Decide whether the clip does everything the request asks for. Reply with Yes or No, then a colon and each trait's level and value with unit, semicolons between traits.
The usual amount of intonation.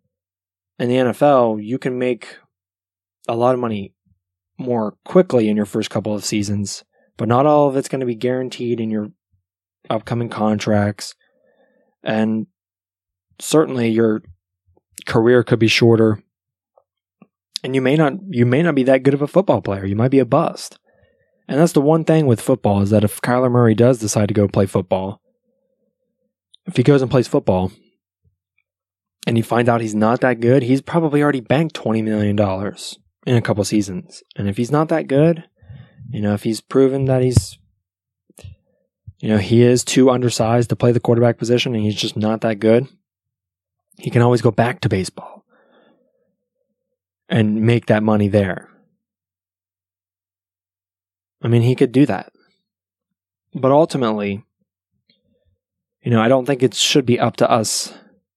Yes: average, 4.5 semitones